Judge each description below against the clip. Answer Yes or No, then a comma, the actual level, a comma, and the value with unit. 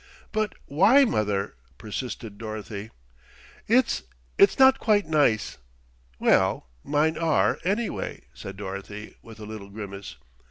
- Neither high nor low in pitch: No, low, 115 Hz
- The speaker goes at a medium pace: No, slow, 115 wpm